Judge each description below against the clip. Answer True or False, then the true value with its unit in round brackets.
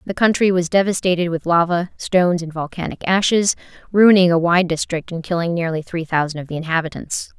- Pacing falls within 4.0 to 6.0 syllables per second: True (5.7 syllables/s)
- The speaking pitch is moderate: True (175 Hz)